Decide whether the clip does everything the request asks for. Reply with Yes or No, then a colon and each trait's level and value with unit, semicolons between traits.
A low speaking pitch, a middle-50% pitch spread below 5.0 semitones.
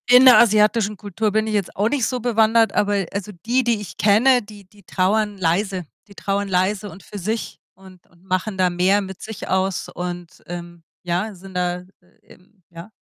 No: high, 200 Hz; average, 2.9 semitones